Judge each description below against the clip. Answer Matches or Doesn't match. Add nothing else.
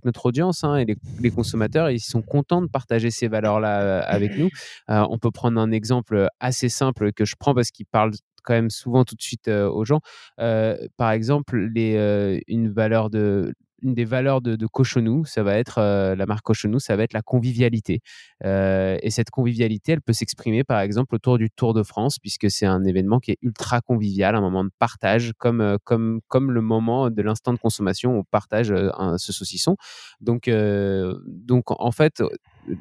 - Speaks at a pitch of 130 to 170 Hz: Doesn't match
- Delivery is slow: Doesn't match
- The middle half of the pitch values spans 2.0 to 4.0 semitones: Matches